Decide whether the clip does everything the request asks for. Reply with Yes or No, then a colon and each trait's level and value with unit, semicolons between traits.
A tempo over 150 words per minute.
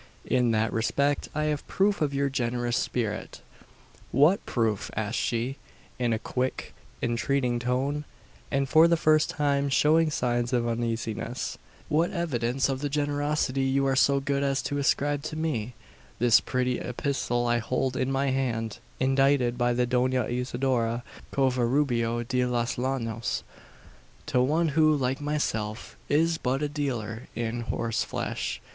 No: average, 145 wpm